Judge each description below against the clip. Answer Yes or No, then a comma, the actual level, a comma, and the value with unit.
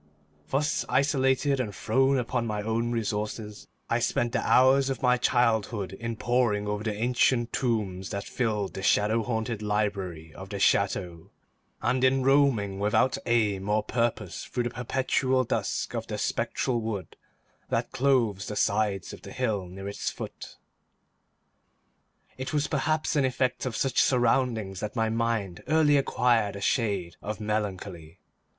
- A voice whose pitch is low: Yes, low, 115 Hz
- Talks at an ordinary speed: Yes, average, 150 wpm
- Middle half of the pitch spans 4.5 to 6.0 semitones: No, average, 3.8 semitones